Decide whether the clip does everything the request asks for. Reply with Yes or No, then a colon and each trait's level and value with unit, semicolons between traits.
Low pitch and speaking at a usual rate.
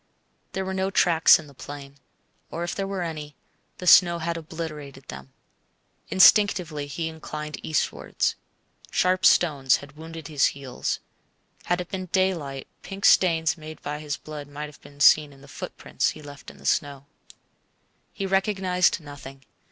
No: medium, 155 Hz; average, 160 wpm